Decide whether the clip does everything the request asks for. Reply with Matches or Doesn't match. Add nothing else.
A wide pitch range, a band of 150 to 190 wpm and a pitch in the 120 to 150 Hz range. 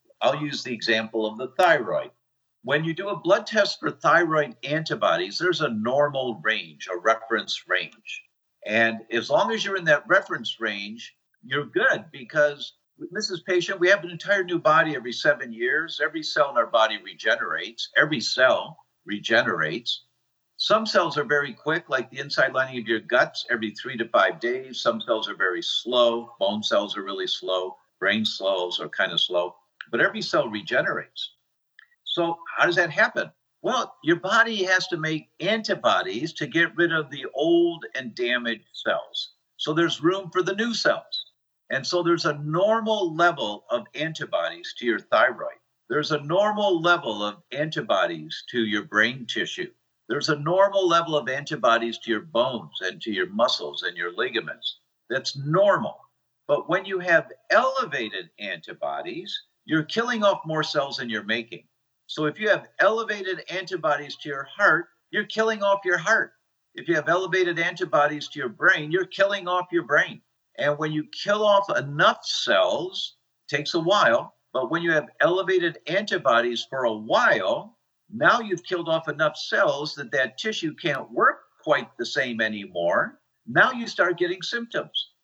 Doesn't match